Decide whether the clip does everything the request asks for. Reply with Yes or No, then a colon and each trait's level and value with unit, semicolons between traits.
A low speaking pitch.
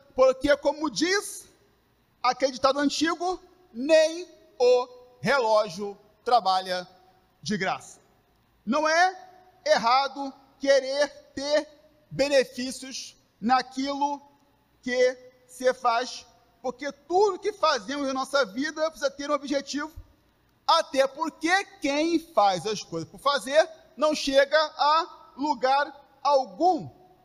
No: very high, 280 Hz